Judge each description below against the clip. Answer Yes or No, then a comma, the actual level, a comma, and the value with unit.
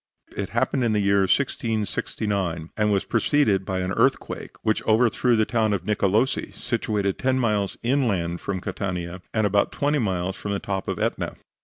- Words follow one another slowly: No, average, 170 wpm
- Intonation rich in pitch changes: No, average, 3.2 semitones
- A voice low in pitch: Yes, low, 105 Hz